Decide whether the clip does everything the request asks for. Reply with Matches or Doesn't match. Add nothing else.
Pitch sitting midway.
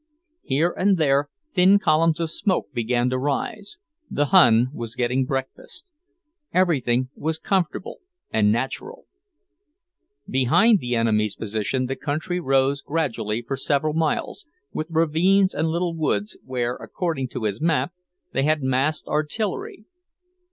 Matches